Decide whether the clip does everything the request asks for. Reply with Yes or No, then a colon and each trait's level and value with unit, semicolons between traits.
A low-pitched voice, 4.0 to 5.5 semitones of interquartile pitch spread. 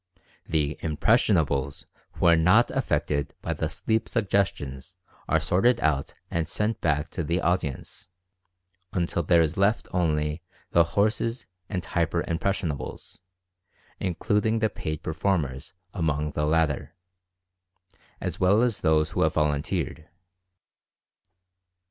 Yes: very low, 85 Hz; average, 4.4 semitones